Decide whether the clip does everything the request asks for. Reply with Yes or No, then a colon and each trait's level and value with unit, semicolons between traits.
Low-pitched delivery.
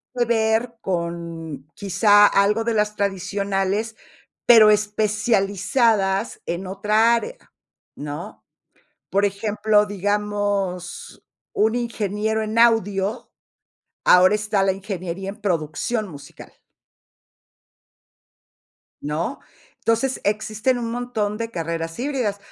No: high, 205 Hz